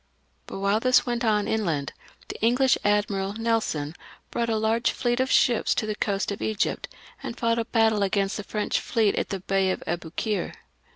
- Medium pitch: No, high, 215 Hz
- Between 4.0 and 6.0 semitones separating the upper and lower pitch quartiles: No, average, 2.7 semitones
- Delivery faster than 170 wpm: Yes, average, 185 wpm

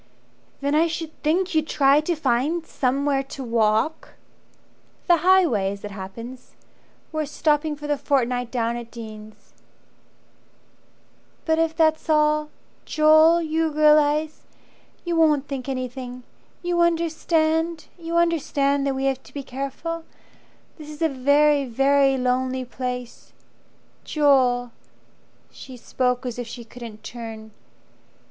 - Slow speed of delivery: Yes, slow, 130 wpm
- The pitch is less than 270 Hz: No, very high, 280 Hz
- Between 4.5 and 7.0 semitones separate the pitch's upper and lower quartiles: No, average, 4.0 semitones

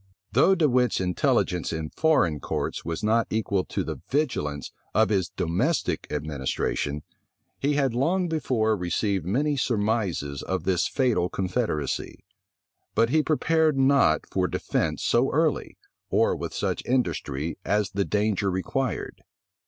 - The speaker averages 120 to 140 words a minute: Yes, slow, 135 wpm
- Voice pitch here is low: Yes, low, 110 Hz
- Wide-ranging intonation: Yes, wide, 7.1 semitones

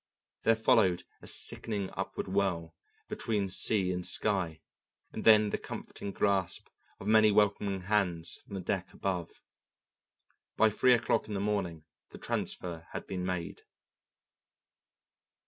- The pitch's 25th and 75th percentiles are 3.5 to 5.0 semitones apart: No, average, 2.7 semitones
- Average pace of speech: No, slow, 130 wpm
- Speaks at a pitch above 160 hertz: No, low, 100 Hz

